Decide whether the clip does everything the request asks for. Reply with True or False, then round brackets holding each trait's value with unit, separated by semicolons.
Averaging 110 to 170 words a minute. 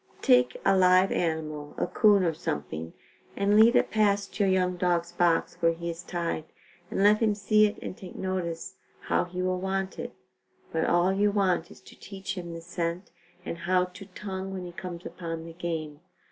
False (200 wpm)